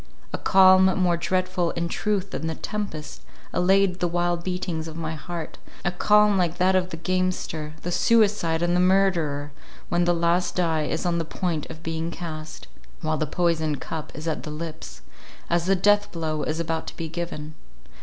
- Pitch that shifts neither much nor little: No, narrow, 2.3 semitones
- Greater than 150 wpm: Yes, average, 175 wpm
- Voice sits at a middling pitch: Yes, medium, 170 Hz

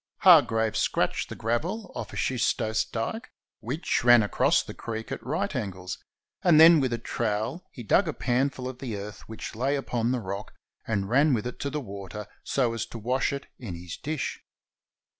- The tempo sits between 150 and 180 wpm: No, average, 190 wpm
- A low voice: Yes, low, 120 Hz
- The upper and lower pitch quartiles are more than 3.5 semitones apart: Yes, average, 4.3 semitones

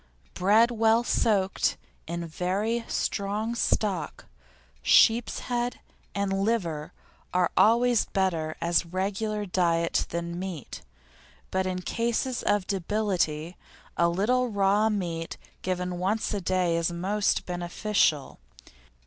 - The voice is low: No, high, 190 Hz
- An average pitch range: Yes, average, 3.9 semitones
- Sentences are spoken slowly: Yes, slow, 110 wpm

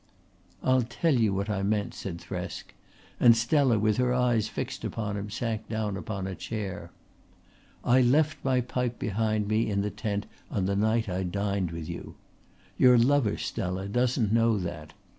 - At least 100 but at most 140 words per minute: No, average, 170 wpm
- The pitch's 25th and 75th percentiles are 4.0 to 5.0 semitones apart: No, average, 3.3 semitones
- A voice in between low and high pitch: No, low, 110 Hz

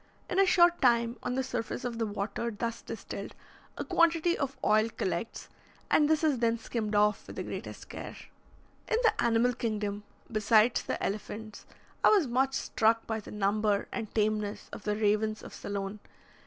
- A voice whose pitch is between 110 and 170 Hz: No, high, 225 Hz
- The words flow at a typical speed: Yes, average, 175 wpm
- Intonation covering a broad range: No, average, 3.0 semitones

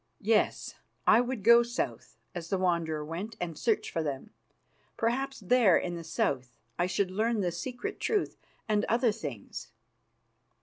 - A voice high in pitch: Yes, high, 195 Hz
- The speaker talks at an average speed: Yes, average, 150 wpm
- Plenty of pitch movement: Yes, wide, 5.8 semitones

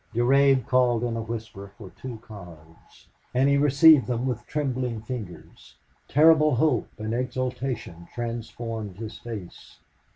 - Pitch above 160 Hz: No, low, 120 Hz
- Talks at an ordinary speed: No, slow, 130 wpm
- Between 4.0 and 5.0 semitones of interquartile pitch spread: No, average, 3.2 semitones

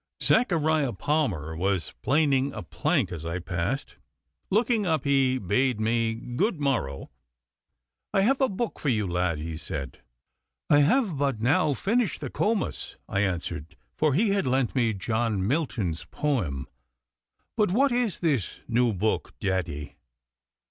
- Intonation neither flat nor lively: No, wide, 9.0 semitones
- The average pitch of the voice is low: Yes, low, 130 Hz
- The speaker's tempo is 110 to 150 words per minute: Yes, average, 140 wpm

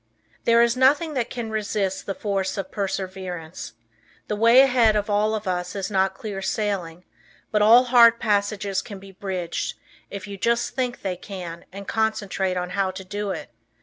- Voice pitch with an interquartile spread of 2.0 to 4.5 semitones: Yes, average, 2.8 semitones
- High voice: Yes, high, 200 Hz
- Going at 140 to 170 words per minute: No, average, 180 wpm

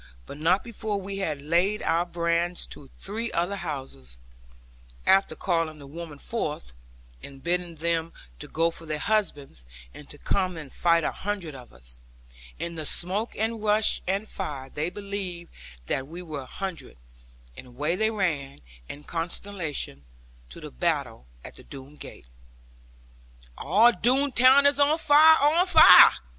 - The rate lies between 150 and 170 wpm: Yes, average, 155 wpm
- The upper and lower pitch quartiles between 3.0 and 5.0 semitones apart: No, wide, 5.5 semitones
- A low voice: No, medium, 170 Hz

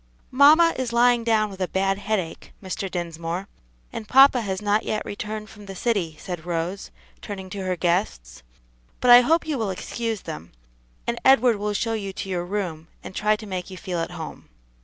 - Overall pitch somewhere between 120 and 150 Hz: No, high, 200 Hz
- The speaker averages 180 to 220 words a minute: Yes, average, 195 wpm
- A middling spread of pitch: Yes, average, 3.9 semitones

